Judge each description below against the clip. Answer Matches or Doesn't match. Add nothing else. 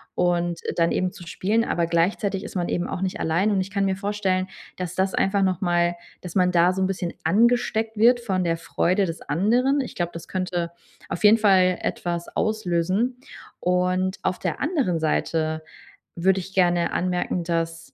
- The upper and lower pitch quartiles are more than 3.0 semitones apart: Doesn't match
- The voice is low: Doesn't match